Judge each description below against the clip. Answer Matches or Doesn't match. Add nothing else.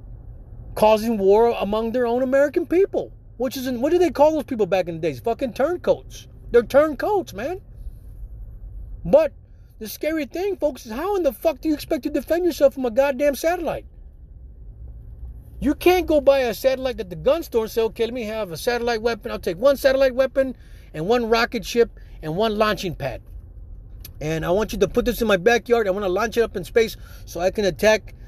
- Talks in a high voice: Matches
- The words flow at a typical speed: Doesn't match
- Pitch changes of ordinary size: Doesn't match